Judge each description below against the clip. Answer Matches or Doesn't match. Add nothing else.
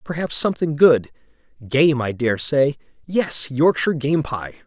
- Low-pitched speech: Doesn't match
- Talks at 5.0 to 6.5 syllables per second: Doesn't match